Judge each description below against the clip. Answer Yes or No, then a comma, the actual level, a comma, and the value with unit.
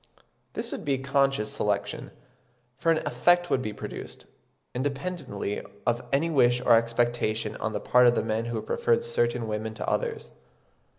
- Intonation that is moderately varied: Yes, average, 4.5 semitones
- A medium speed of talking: Yes, average, 160 wpm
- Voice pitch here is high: No, low, 125 Hz